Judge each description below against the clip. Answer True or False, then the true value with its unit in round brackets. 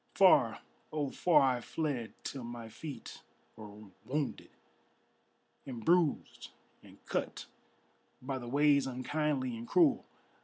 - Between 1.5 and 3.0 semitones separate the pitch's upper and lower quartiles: False (3.8 semitones)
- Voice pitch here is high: False (135 Hz)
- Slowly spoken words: True (115 wpm)